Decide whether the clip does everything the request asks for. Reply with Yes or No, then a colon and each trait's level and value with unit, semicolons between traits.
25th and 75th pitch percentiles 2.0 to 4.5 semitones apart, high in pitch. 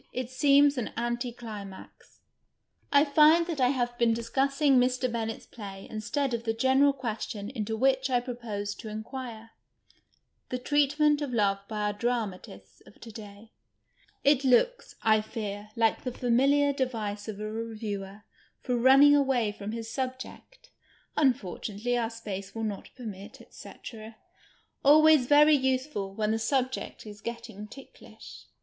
Yes: average, 3.9 semitones; high, 235 Hz